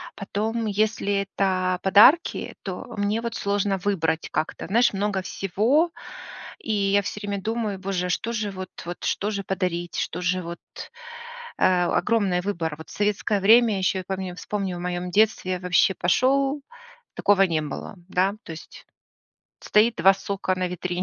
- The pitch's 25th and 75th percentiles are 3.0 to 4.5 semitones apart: No, narrow, 2.6 semitones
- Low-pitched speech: No, high, 195 Hz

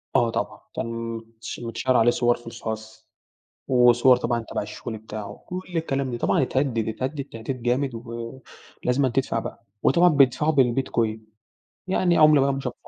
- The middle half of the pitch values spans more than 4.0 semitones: No, average, 2.7 semitones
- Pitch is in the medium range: No, low, 120 Hz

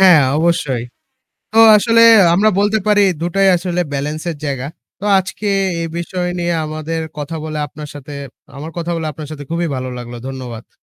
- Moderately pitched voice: Yes, medium, 160 Hz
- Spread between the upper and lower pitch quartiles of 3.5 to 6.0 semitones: Yes, average, 3.9 semitones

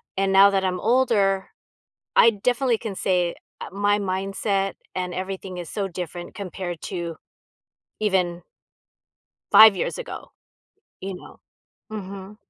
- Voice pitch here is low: No, high, 195 Hz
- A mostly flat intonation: Yes, narrow, 1.9 semitones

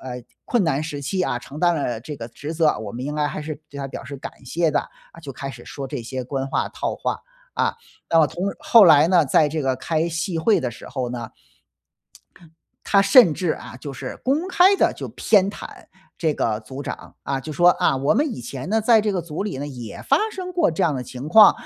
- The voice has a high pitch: No, medium, 150 Hz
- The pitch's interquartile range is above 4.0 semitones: Yes, wide, 5.6 semitones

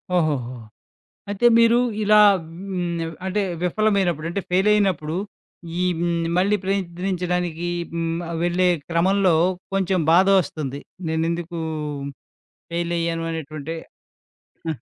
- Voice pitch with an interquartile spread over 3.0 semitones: No, narrow, 2.6 semitones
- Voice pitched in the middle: Yes, medium, 175 Hz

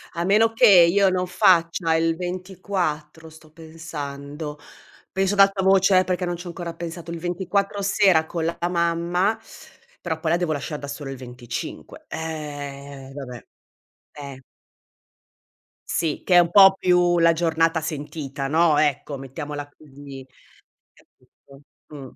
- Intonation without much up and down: No, average, 3.5 semitones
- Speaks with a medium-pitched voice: Yes, medium, 165 Hz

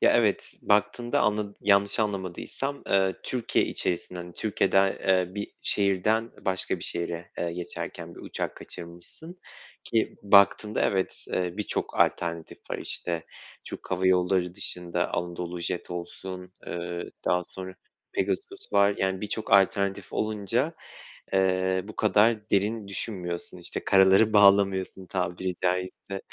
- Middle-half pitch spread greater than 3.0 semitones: No, narrow, 2.5 semitones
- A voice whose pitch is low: Yes, very low, 95 Hz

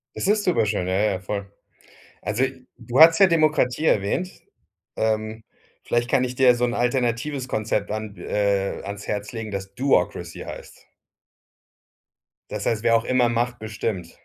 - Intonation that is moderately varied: Yes, average, 3.6 semitones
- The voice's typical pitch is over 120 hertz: No, low, 115 Hz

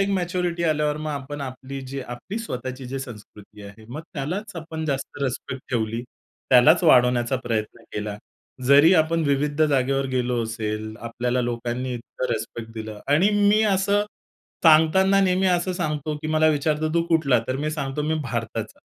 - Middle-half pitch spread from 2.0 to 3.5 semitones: No, average, 4.7 semitones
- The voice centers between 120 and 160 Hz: Yes, medium, 140 Hz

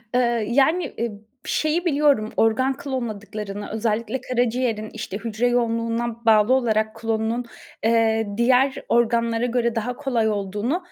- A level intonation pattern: Yes, narrow, 2.2 semitones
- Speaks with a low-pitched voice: No, high, 230 Hz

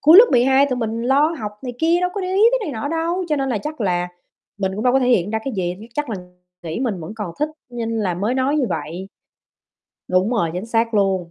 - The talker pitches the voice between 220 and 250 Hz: Yes, high, 240 Hz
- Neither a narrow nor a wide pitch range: No, wide, 6.6 semitones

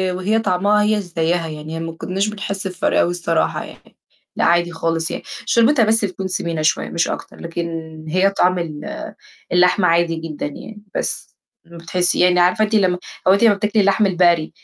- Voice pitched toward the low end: No, medium, 180 Hz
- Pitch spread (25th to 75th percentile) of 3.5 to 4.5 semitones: No, average, 3.1 semitones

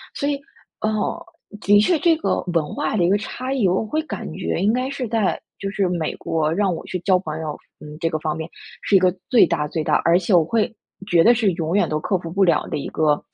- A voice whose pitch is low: No, high, 190 Hz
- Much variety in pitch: No, average, 4.9 semitones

